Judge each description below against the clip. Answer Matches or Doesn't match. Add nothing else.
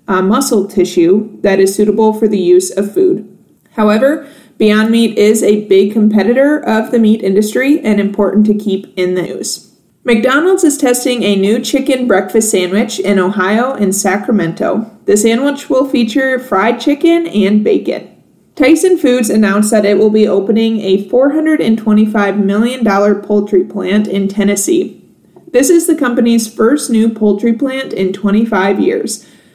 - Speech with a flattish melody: Doesn't match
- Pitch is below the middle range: Doesn't match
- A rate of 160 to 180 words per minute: Doesn't match